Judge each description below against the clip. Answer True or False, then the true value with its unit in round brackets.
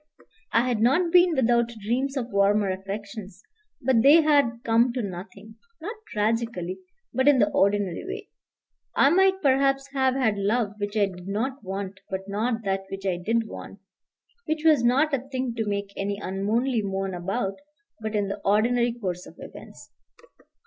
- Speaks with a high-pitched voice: True (225 Hz)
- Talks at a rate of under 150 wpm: False (170 wpm)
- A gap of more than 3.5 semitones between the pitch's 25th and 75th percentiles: True (4.8 semitones)